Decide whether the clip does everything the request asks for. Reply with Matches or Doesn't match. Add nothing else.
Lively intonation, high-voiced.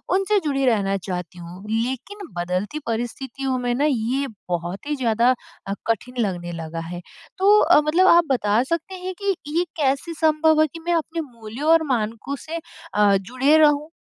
Matches